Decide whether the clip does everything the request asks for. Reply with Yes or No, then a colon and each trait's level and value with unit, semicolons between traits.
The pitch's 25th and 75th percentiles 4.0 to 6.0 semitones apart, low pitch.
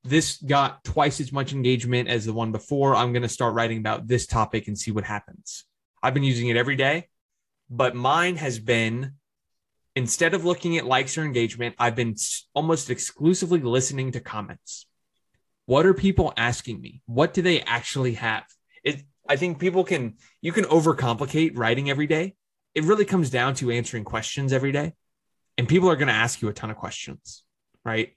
Yes: average, 4.9 semitones; low, 130 Hz